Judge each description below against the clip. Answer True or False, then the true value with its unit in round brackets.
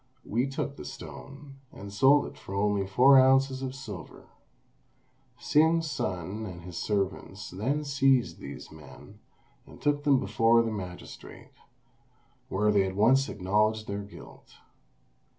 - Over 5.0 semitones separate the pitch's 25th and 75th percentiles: True (5.6 semitones)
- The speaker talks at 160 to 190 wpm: False (135 wpm)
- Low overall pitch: True (110 Hz)